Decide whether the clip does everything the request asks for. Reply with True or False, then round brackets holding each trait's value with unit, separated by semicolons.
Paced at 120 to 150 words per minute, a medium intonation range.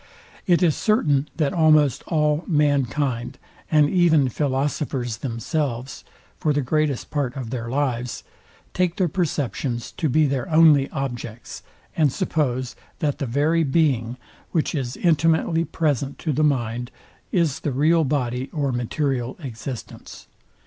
True (135 wpm; 3.8 semitones)